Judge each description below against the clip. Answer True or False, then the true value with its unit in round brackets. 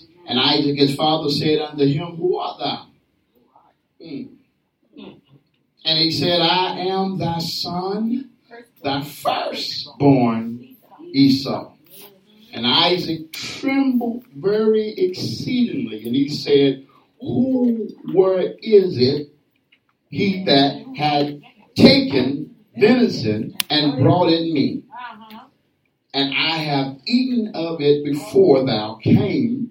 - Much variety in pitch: True (8.0 semitones)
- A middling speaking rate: False (100 wpm)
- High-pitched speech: False (165 Hz)